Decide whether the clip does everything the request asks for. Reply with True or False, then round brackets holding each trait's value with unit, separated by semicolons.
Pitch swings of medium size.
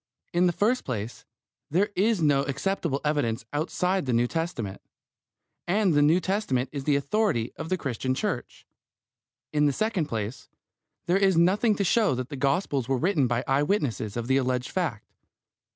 False (6.5 semitones)